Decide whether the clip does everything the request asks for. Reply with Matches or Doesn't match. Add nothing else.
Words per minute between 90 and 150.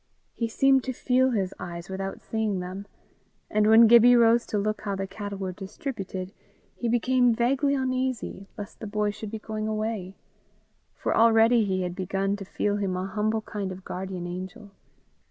Doesn't match